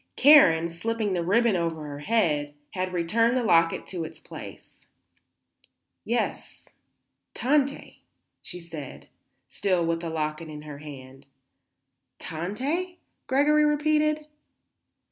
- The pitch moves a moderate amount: No, wide, 8.1 semitones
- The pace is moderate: No, slow, 110 wpm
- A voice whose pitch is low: No, medium, 180 Hz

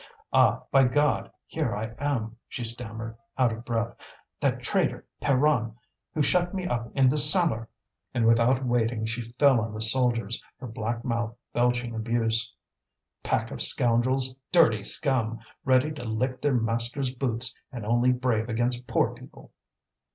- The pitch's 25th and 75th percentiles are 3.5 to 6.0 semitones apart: No, narrow, 2.4 semitones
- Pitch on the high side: No, low, 120 Hz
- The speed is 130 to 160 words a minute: Yes, average, 150 wpm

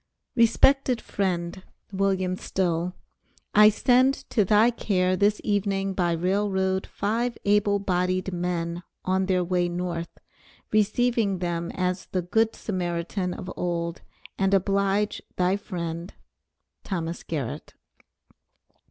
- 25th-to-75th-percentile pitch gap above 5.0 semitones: No, narrow, 2.5 semitones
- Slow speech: Yes, slow, 115 wpm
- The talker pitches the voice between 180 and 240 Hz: Yes, high, 190 Hz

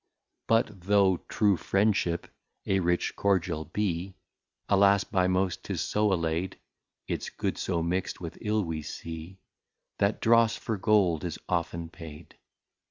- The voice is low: Yes, very low, 95 Hz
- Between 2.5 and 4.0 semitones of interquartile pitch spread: Yes, average, 3.1 semitones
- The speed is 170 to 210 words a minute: No, slow, 135 wpm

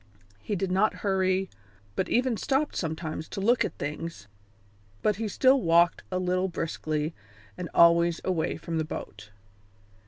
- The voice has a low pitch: No, medium, 180 Hz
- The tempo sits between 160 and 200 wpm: No, average, 150 wpm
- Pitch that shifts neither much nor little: Yes, average, 3.5 semitones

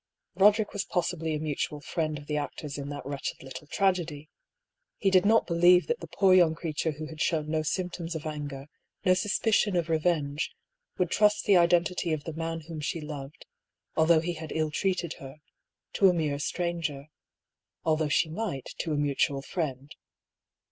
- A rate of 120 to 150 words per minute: No, average, 175 wpm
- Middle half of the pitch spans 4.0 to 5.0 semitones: No, average, 3.0 semitones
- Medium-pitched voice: Yes, medium, 160 Hz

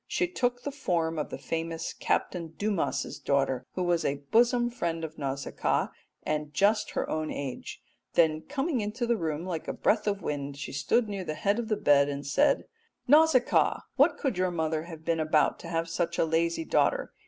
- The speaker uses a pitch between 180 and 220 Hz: No, medium, 170 Hz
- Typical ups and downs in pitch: No, wide, 5.9 semitones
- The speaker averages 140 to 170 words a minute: No, average, 195 wpm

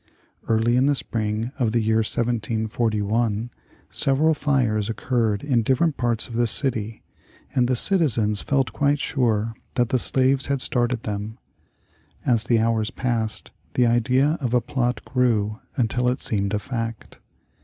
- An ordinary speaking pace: Yes, average, 150 wpm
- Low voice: Yes, low, 120 Hz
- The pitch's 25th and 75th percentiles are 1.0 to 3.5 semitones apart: Yes, average, 2.7 semitones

